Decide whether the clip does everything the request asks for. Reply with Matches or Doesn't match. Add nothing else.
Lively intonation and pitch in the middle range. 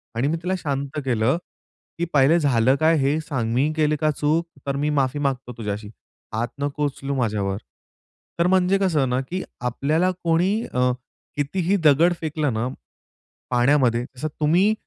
Doesn't match